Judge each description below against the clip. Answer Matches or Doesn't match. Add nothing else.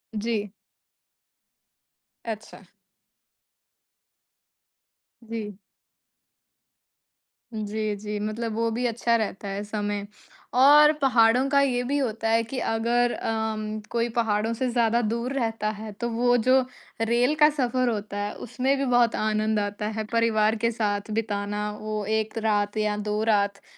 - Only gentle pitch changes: Matches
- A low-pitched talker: Doesn't match